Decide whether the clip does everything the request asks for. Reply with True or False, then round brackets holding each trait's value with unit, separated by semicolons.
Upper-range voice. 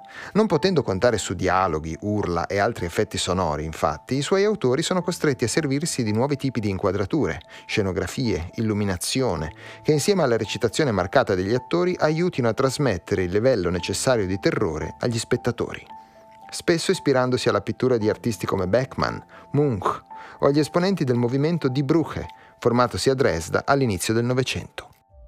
False (120 Hz)